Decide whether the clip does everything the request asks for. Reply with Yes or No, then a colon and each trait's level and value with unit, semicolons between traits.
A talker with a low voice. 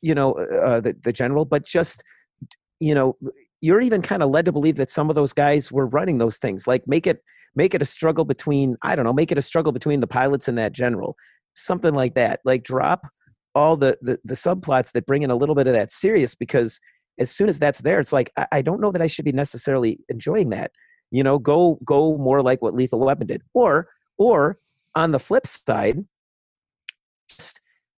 No: medium, 145 Hz